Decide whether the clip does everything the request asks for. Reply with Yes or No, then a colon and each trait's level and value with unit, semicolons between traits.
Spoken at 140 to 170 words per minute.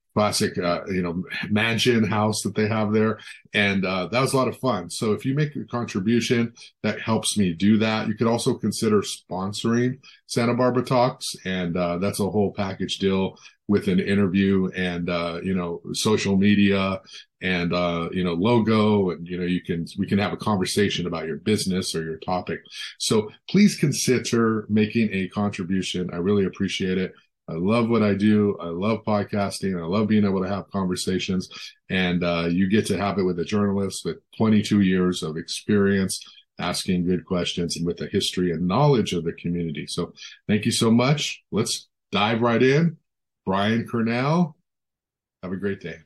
No: average, 185 wpm